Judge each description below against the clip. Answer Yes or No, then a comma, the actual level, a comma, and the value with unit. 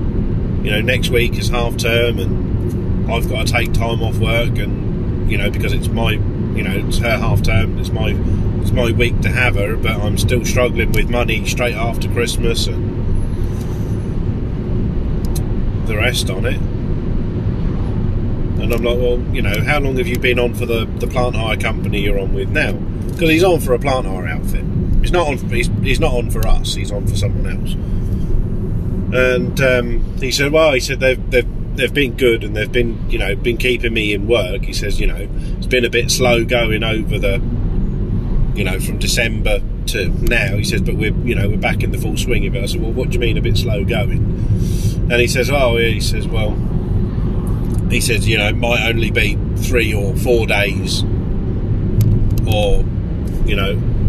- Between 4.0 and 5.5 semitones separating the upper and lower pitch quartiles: No, average, 3.3 semitones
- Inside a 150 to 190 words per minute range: No, average, 200 wpm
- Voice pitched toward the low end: Yes, low, 110 Hz